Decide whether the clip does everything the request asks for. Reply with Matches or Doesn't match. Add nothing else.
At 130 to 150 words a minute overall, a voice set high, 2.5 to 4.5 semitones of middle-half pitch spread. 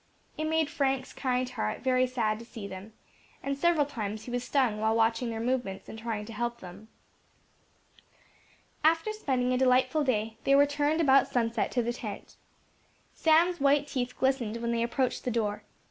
Doesn't match